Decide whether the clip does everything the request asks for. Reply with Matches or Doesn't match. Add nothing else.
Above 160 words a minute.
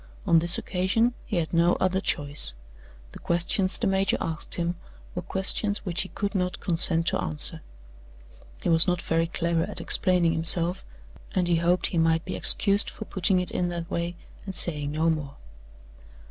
Matches